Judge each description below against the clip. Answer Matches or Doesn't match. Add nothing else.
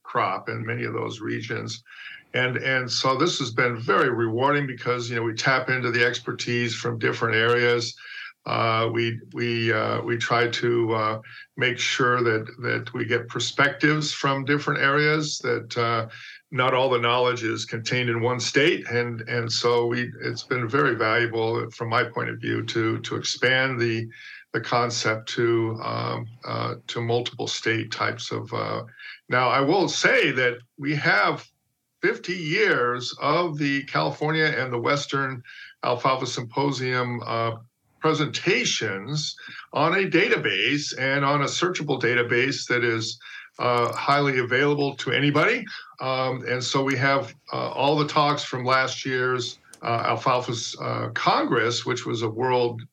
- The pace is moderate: Matches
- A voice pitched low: Matches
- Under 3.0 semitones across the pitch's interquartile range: Matches